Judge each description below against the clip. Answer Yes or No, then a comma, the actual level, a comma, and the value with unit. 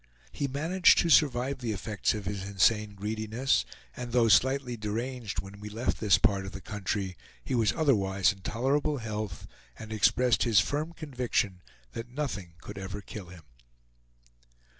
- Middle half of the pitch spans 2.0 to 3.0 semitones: No, average, 4.3 semitones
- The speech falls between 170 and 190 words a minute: No, average, 160 wpm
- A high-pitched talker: No, low, 110 Hz